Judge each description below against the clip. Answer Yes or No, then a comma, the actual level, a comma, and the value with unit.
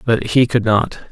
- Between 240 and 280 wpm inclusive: No, fast, 215 wpm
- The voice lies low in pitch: Yes, low, 115 Hz